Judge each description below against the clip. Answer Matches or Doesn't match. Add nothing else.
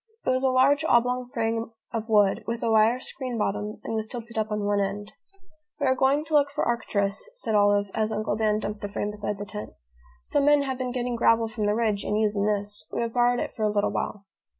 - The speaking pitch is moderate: Doesn't match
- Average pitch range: Matches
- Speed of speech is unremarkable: Doesn't match